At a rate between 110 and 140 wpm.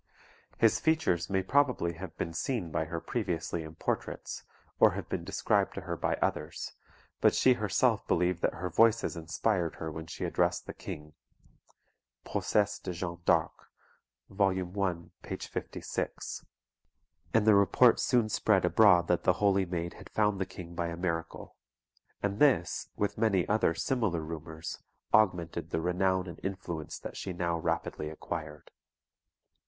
No: average, 155 wpm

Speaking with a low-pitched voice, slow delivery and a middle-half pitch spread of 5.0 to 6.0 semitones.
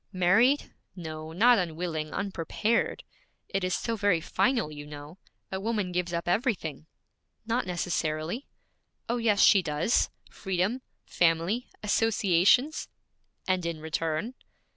No: medium, 180 Hz; slow, 120 wpm; average, 5.3 semitones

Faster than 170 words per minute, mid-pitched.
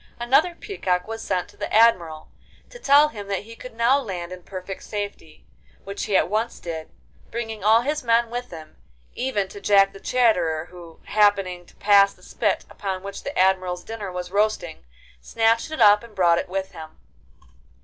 No: average, 185 wpm; high, 200 Hz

